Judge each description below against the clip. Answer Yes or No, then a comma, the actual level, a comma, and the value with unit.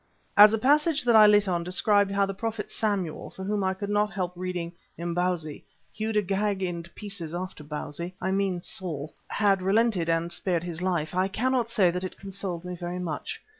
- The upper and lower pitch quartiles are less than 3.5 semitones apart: Yes, average, 3.1 semitones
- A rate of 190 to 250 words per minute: Yes, average, 195 wpm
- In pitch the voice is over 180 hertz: Yes, high, 190 Hz